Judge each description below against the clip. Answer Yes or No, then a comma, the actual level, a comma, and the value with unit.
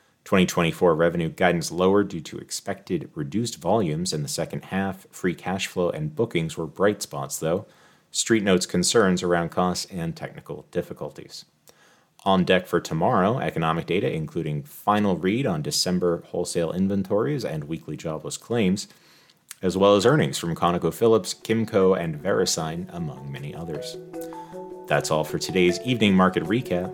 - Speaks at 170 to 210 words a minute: No, average, 145 wpm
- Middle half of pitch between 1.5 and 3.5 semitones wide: No, average, 4.8 semitones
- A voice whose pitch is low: Yes, very low, 95 Hz